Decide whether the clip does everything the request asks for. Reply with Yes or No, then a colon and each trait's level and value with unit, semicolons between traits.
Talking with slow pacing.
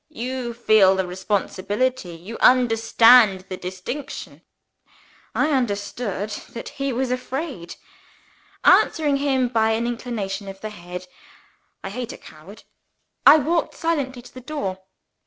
Yes: slow, 125 wpm